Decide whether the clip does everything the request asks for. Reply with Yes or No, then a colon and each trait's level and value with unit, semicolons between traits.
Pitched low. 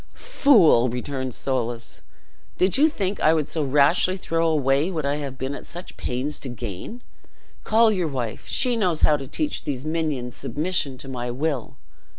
No: medium, 145 Hz